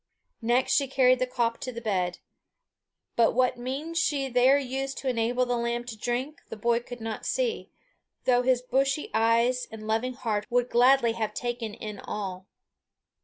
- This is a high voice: Yes, high, 245 Hz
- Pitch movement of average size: No, narrow, 2.3 semitones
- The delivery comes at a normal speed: Yes, average, 170 wpm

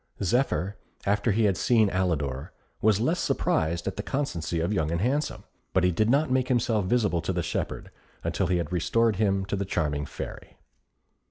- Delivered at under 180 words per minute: No, average, 185 wpm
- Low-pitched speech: Yes, low, 100 Hz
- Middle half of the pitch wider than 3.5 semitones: Yes, average, 5.0 semitones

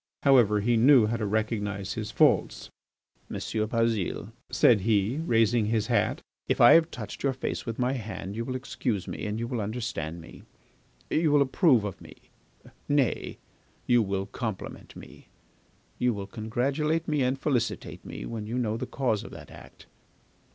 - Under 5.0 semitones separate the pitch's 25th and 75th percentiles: Yes, average, 3.4 semitones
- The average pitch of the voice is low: Yes, low, 115 Hz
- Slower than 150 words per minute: No, average, 170 wpm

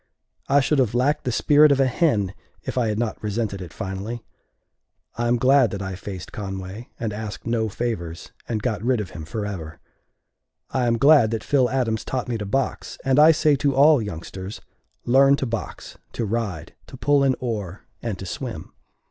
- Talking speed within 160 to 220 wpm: Yes, average, 190 wpm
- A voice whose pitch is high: No, low, 115 Hz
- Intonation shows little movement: No, average, 4.6 semitones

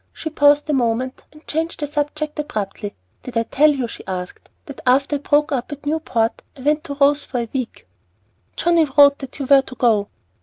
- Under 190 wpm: No, fast, 205 wpm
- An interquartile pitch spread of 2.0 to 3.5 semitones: Yes, average, 3.0 semitones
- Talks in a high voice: Yes, very high, 280 Hz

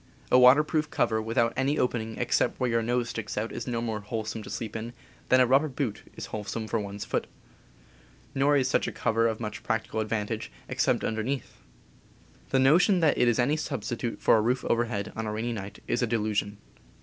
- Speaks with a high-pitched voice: No, low, 115 Hz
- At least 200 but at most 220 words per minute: Yes, fast, 205 wpm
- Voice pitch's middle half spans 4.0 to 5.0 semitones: No, narrow, 2.6 semitones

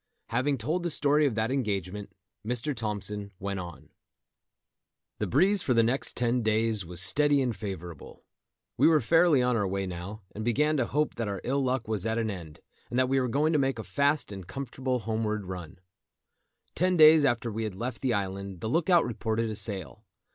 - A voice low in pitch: Yes, low, 115 Hz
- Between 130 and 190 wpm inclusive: No, average, 200 wpm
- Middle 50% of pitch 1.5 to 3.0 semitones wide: No, average, 5.3 semitones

